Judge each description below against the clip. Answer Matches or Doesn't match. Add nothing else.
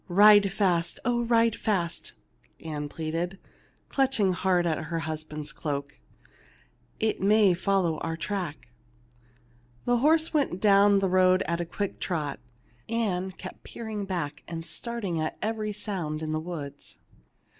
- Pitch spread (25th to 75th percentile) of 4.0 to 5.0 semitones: Matches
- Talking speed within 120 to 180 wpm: Matches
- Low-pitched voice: Doesn't match